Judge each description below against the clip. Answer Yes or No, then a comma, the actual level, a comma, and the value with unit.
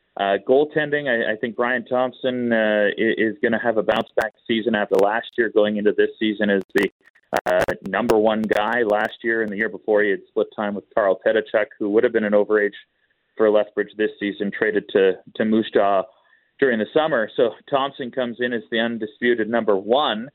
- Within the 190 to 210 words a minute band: Yes, fast, 205 wpm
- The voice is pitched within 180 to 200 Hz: No, low, 110 Hz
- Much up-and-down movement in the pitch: No, average, 2.8 semitones